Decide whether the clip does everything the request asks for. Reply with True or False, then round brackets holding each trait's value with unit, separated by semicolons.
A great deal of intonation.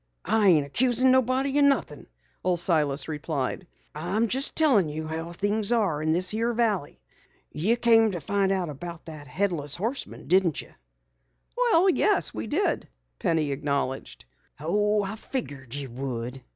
True (7.3 semitones)